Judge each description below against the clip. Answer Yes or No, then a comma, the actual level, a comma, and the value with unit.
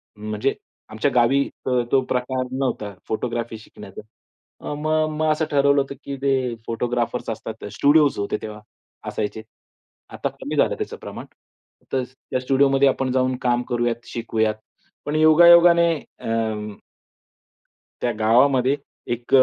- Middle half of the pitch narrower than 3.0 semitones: No, average, 3.4 semitones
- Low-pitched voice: Yes, low, 125 Hz